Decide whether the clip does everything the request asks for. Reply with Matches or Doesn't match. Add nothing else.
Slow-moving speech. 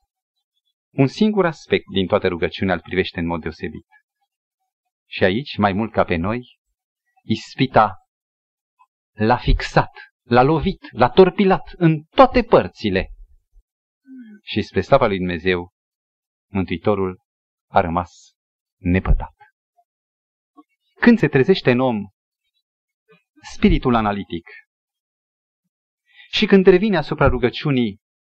Matches